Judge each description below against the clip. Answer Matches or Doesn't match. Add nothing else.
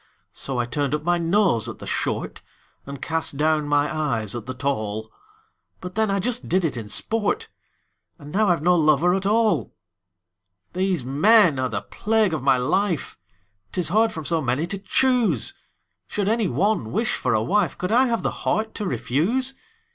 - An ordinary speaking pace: Matches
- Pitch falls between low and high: Matches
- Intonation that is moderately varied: Doesn't match